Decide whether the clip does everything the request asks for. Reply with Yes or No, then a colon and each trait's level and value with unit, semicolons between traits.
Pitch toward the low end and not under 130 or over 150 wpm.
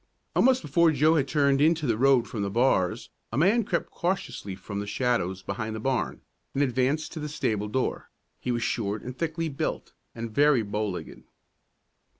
No: low, 130 Hz; average, 180 wpm